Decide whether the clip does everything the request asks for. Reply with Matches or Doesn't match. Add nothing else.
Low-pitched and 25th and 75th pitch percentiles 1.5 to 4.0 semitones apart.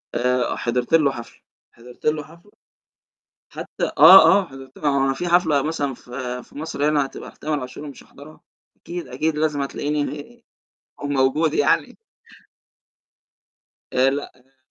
Doesn't match